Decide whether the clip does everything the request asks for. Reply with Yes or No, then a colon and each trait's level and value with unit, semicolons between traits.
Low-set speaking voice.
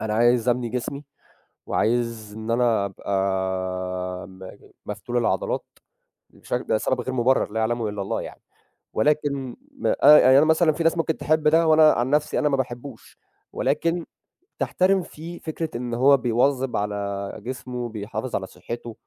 Yes: low, 120 Hz